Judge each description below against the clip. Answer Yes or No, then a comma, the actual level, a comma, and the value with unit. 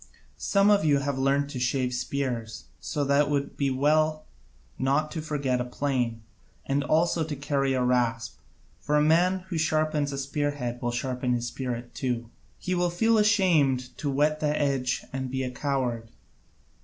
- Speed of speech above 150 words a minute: Yes, average, 180 wpm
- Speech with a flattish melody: No, average, 3.4 semitones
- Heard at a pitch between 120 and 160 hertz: Yes, medium, 140 Hz